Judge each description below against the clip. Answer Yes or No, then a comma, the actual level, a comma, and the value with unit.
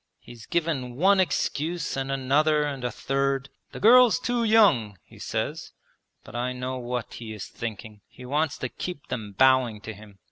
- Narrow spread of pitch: No, average, 4.6 semitones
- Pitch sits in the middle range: No, low, 130 Hz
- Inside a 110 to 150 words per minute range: No, average, 175 wpm